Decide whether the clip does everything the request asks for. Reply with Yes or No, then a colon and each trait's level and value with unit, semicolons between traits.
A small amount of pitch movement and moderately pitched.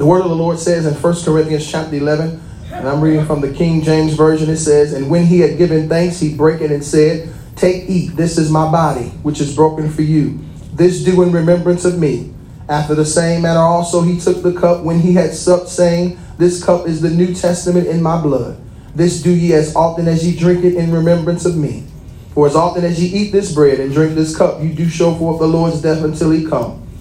Yes: narrow, 2.1 semitones; medium, 165 Hz